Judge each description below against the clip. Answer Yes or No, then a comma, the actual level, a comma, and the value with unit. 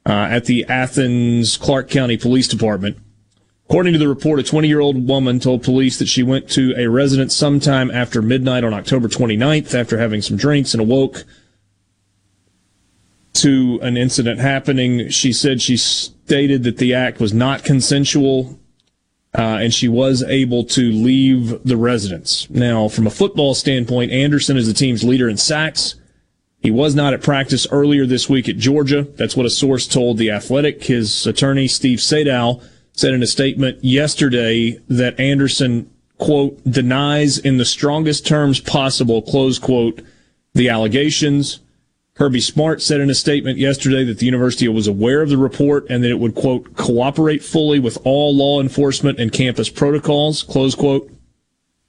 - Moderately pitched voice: No, low, 130 Hz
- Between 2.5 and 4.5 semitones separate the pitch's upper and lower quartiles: Yes, average, 3.0 semitones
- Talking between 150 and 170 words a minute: Yes, average, 165 wpm